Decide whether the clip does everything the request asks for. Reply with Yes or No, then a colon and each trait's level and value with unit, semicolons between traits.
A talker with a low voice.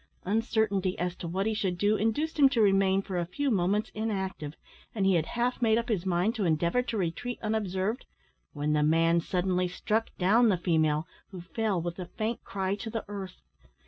No: high, 195 Hz